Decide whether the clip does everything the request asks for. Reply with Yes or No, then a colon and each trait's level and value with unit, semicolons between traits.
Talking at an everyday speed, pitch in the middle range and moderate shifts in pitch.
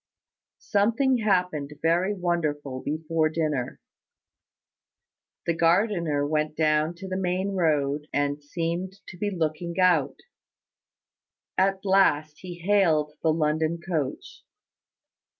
No: slow, 105 wpm; medium, 165 Hz; average, 3.5 semitones